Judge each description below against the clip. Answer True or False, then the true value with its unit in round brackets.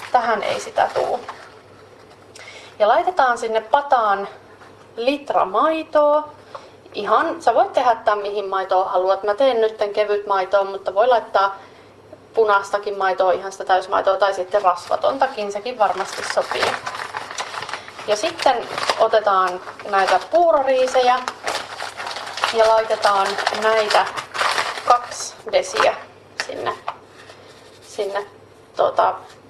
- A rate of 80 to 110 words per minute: True (100 wpm)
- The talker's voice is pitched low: False (210 Hz)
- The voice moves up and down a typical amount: True (4.7 semitones)